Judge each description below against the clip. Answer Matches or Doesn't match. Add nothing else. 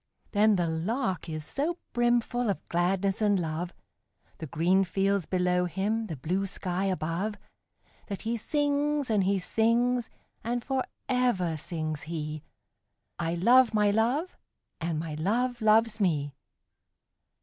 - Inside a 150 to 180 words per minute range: Doesn't match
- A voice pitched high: Matches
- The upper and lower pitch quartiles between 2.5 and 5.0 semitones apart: Doesn't match